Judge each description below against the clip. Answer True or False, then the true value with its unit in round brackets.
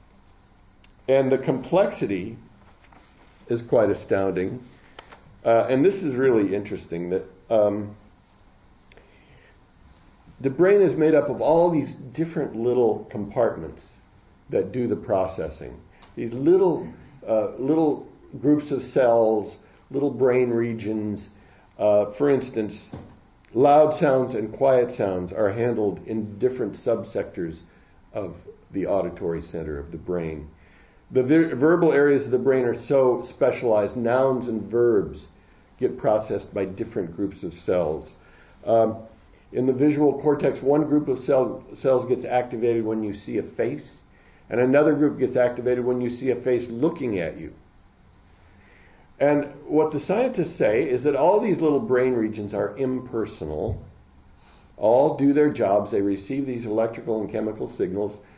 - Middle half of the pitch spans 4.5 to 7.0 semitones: True (5.3 semitones)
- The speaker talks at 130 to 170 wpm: True (140 wpm)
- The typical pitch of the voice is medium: False (120 Hz)